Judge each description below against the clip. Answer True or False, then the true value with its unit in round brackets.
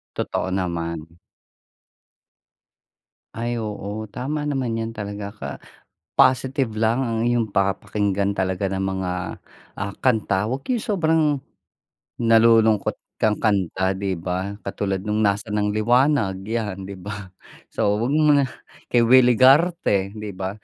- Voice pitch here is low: True (105 Hz)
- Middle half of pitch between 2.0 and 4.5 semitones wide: True (3.7 semitones)